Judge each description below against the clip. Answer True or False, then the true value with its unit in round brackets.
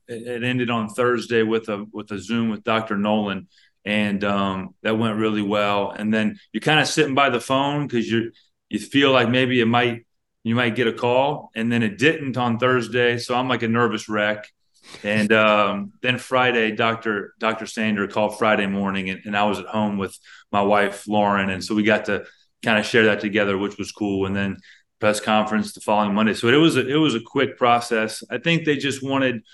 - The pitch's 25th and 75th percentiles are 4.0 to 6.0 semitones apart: False (2.9 semitones)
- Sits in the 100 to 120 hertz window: True (110 Hz)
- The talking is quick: True (215 wpm)